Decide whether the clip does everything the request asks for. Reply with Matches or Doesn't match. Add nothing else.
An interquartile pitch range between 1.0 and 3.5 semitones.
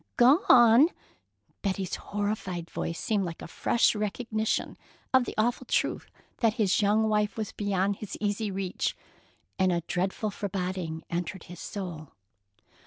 Matches